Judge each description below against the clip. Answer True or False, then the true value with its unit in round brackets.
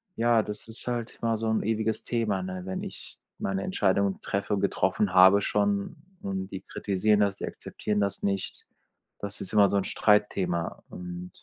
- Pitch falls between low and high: False (100 Hz)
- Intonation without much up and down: True (2.1 semitones)